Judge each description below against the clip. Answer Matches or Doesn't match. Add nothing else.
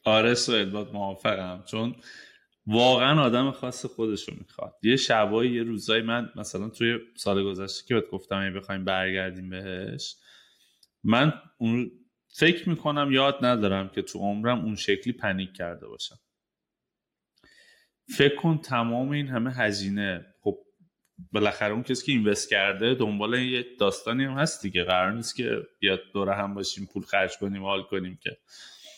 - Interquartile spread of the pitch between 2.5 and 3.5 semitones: Doesn't match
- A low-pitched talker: Matches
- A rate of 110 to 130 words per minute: Doesn't match